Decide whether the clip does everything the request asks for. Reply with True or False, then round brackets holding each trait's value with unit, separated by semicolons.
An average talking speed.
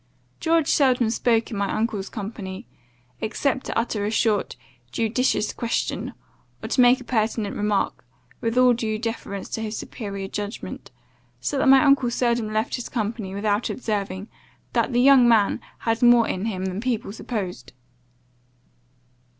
True (150 wpm)